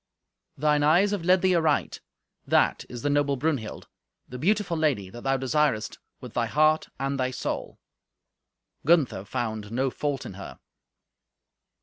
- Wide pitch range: No, average, 4.3 semitones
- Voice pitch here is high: No, medium, 140 Hz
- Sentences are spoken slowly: No, average, 145 wpm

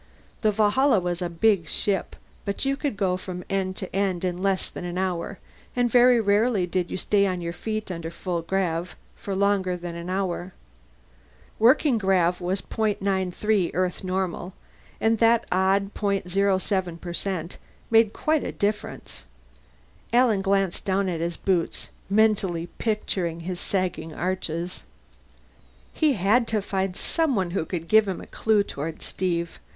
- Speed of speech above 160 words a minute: No, average, 150 wpm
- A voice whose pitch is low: No, high, 190 Hz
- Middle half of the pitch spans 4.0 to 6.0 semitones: No, average, 2.9 semitones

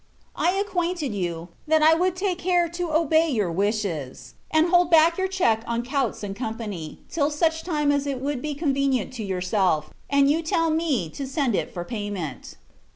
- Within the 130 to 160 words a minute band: No, average, 190 wpm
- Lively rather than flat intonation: Yes, wide, 7.8 semitones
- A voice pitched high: Yes, very high, 280 Hz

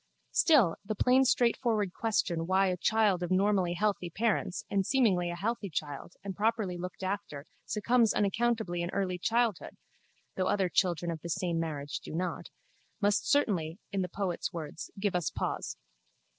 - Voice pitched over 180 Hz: Yes, high, 190 Hz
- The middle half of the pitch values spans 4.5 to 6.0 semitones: No, average, 3.6 semitones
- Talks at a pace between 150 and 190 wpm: Yes, average, 160 wpm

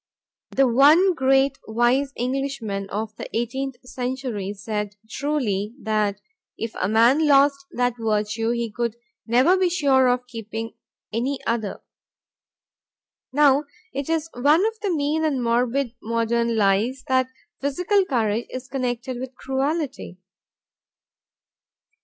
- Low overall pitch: No, very high, 250 Hz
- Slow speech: Yes, slow, 125 wpm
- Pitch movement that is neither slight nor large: Yes, average, 3.6 semitones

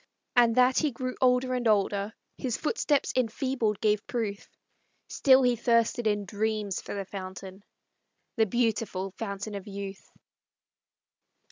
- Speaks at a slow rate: Yes, slow, 130 wpm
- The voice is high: Yes, high, 220 Hz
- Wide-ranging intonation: No, average, 3.8 semitones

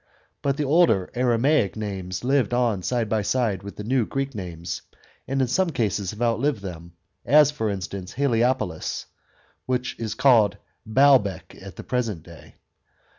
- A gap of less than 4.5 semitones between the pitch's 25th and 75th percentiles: No, average, 5.1 semitones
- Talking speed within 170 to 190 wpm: No, average, 155 wpm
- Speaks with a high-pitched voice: No, low, 115 Hz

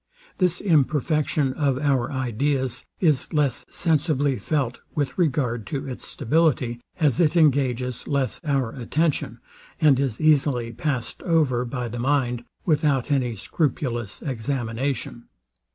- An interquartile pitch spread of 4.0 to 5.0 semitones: No, average, 3.6 semitones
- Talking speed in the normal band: No, slow, 120 wpm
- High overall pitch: No, low, 135 Hz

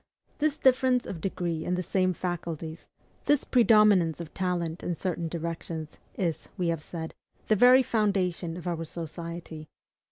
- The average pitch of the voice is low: No, medium, 175 Hz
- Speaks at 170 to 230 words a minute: No, average, 150 wpm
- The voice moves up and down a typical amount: Yes, average, 3.4 semitones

